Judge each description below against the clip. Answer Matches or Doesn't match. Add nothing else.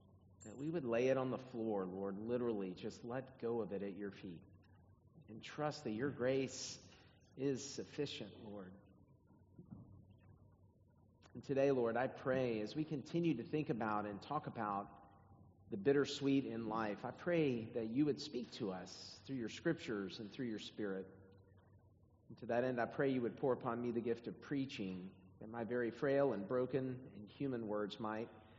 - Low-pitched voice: Matches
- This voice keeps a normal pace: Matches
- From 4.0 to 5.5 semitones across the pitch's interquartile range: Matches